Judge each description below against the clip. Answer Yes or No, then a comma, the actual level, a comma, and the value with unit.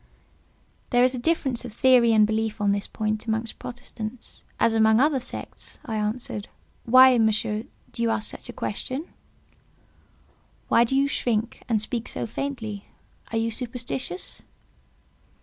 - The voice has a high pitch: Yes, high, 230 Hz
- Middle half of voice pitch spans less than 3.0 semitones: Yes, narrow, 2.6 semitones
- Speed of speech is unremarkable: Yes, average, 150 wpm